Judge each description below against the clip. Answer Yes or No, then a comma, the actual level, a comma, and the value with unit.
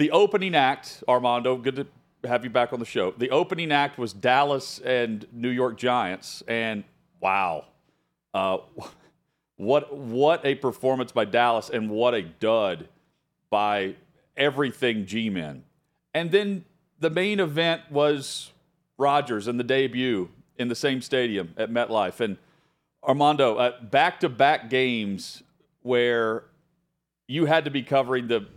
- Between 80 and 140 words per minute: Yes, slow, 135 wpm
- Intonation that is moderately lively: Yes, average, 4.0 semitones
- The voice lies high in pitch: No, low, 130 Hz